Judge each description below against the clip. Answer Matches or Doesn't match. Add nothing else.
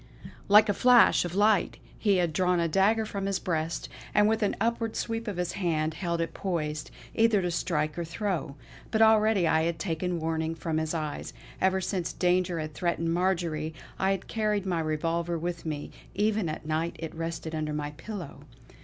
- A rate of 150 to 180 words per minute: Doesn't match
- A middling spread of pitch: Matches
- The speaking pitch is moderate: Matches